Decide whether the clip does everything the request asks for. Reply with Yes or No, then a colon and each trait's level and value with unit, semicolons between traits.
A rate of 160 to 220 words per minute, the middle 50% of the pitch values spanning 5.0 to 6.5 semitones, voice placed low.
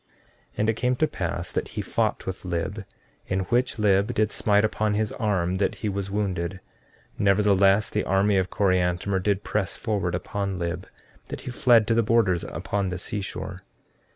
No: average, 180 wpm; narrow, 2.4 semitones; low, 100 Hz